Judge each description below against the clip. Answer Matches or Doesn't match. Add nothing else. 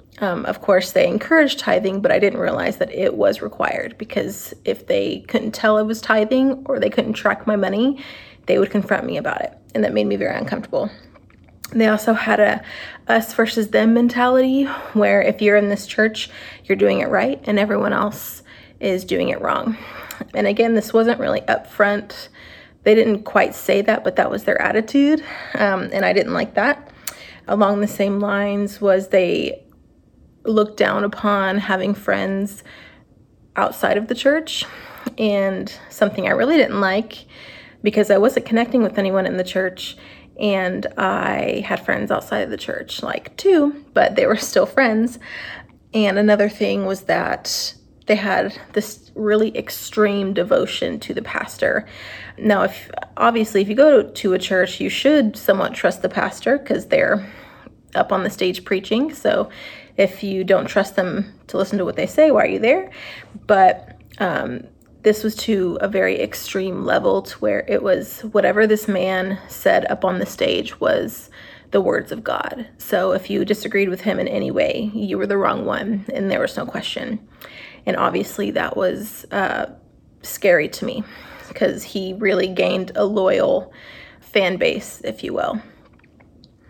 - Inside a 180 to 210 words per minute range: Doesn't match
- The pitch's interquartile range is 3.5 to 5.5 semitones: Doesn't match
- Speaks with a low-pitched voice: Doesn't match